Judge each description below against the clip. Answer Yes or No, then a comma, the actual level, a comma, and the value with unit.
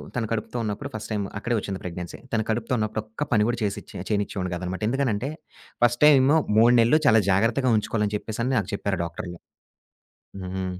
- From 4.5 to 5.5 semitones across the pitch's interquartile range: No, average, 3.2 semitones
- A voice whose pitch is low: Yes, low, 110 Hz